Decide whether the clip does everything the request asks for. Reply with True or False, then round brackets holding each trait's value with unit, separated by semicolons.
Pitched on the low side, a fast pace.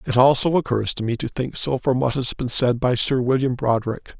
True (125 Hz; 245 wpm)